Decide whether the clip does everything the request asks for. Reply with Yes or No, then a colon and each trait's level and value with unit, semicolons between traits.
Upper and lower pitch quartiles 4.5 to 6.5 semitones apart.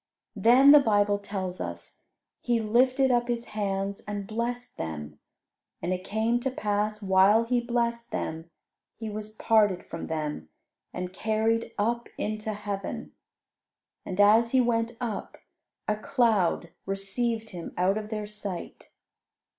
No: average, 3.1 semitones